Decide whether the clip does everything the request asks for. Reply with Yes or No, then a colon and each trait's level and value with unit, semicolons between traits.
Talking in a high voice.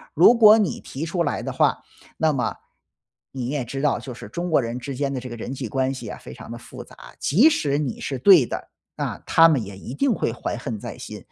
No: low, 135 Hz